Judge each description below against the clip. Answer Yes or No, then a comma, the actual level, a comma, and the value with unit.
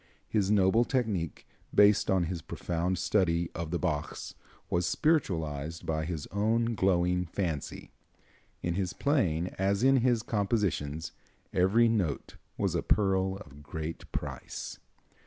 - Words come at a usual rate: No, slow, 130 wpm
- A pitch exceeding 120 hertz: No, very low, 95 Hz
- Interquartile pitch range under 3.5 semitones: No, average, 4.1 semitones